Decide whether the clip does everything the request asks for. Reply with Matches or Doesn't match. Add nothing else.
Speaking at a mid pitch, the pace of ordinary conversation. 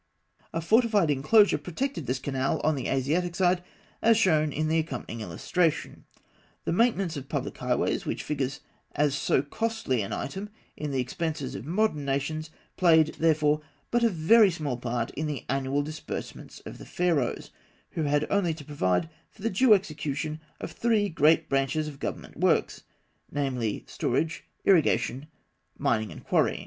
Matches